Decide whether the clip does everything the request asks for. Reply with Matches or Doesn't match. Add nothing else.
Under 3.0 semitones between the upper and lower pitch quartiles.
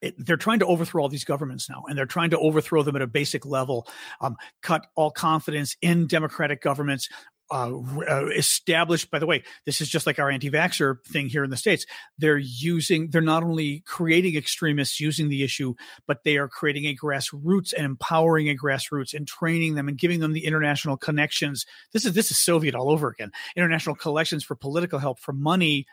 Matches